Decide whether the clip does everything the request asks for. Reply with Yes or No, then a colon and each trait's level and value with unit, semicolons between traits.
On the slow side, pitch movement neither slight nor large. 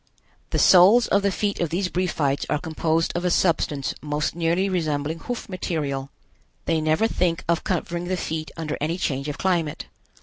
No: average, 175 wpm; average, 3.1 semitones